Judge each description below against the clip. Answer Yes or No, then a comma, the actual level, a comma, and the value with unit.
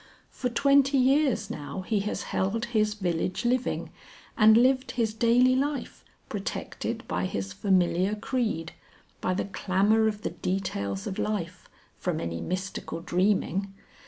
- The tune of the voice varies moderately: Yes, average, 4.6 semitones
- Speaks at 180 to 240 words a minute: No, slow, 135 wpm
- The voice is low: No, high, 210 Hz